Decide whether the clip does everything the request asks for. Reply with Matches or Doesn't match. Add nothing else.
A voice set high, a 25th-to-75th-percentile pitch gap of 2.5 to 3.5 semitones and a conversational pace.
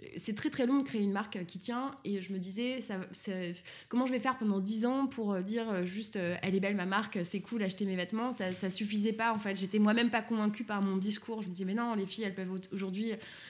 Doesn't match